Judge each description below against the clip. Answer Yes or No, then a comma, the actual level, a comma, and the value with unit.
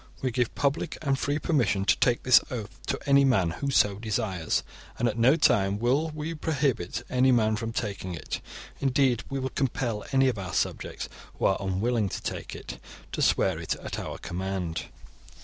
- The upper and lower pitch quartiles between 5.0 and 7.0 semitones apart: Yes, average, 5.3 semitones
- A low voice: Yes, low, 120 Hz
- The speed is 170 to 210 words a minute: Yes, average, 185 wpm